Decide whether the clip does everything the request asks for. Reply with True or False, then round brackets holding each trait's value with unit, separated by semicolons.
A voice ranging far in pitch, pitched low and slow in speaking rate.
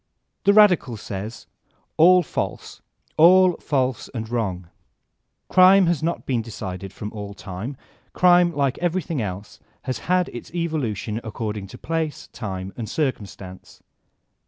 True (8.5 semitones; 125 Hz; 130 wpm)